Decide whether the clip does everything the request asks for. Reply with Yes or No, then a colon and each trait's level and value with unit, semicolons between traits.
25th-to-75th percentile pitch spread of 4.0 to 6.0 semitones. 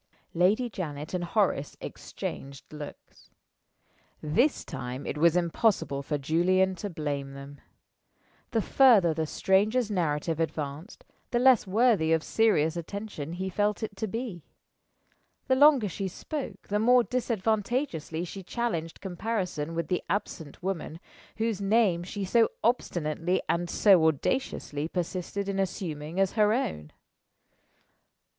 Yes: wide, 5.4 semitones